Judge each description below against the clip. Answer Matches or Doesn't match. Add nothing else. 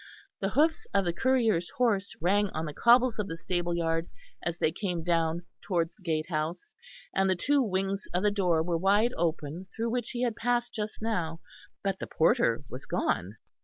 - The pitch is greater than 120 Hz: Matches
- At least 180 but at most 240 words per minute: Matches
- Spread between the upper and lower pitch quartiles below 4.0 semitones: Doesn't match